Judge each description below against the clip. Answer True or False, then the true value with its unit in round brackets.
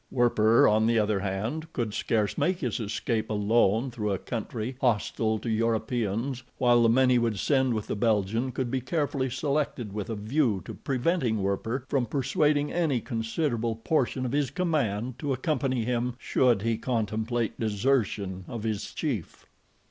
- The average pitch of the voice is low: True (120 Hz)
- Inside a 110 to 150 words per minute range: False (165 wpm)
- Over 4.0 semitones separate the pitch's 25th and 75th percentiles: False (3.3 semitones)